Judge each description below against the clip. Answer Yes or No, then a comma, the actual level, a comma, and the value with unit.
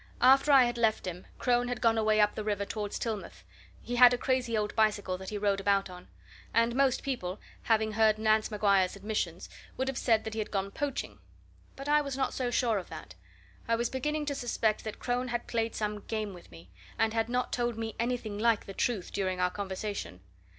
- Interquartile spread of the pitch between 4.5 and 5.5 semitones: No, average, 3.1 semitones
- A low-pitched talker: No, high, 220 Hz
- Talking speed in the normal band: No, fast, 215 wpm